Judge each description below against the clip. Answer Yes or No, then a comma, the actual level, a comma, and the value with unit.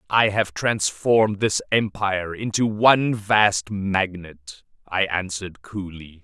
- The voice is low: Yes, low, 100 Hz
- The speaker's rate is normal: No, slow, 115 wpm